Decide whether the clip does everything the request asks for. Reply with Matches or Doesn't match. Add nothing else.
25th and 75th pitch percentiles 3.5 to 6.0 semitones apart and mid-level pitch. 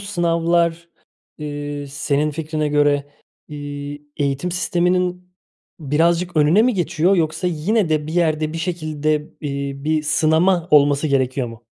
Doesn't match